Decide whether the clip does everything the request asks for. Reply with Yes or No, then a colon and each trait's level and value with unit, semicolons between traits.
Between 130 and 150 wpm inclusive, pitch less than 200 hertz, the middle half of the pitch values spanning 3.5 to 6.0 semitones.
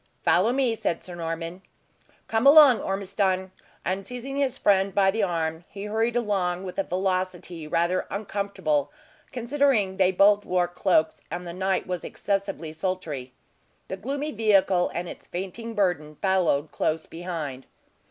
No: average, 145 wpm; high, 190 Hz; average, 3.1 semitones